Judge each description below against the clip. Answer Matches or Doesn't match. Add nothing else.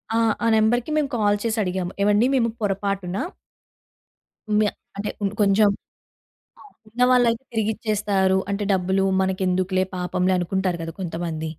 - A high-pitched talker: Matches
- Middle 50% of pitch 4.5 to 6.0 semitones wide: Doesn't match